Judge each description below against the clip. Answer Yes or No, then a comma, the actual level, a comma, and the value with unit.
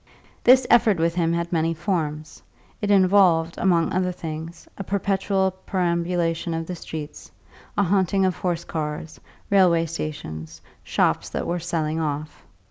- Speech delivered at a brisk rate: No, average, 140 wpm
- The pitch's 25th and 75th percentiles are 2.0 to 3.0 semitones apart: Yes, average, 2.7 semitones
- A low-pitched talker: No, medium, 170 Hz